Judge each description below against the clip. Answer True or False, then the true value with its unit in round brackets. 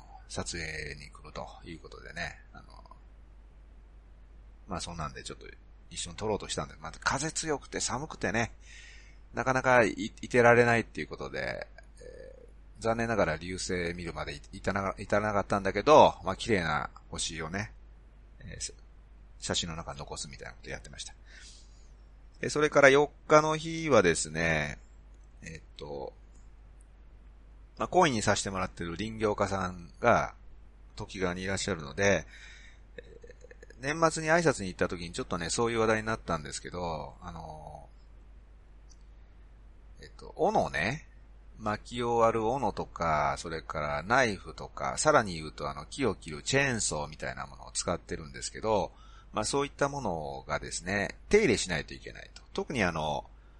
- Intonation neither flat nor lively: False (6.5 semitones)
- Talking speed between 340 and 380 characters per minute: False (315 characters per minute)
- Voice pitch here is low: True (95 Hz)